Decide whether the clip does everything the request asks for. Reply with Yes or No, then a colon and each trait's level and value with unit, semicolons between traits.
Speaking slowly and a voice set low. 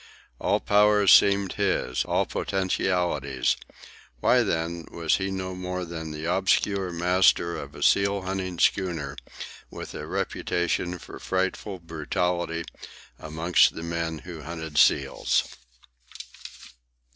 Yes: slow, 110 wpm; very low, 90 Hz